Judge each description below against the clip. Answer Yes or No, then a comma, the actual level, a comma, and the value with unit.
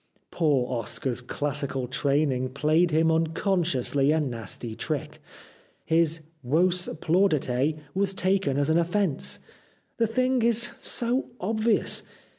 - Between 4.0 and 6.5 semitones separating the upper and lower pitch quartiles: Yes, wide, 5.5 semitones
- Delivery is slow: Yes, slow, 120 wpm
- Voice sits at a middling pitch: Yes, medium, 160 Hz